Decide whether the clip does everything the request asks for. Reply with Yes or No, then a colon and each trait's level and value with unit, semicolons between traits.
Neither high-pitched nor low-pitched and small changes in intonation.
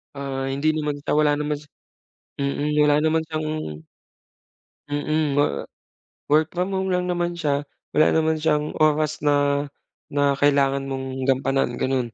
Yes: medium, 145 Hz; narrow, 2.0 semitones